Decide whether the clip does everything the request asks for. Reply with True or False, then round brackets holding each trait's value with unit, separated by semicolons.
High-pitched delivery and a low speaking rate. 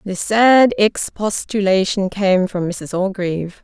True (195 Hz; 115 wpm)